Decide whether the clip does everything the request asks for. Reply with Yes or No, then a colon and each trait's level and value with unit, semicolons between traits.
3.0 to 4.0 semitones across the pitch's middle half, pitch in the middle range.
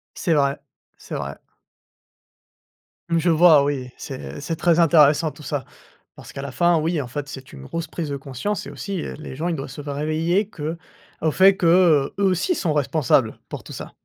Yes: average, 3.5 semitones; medium, 155 Hz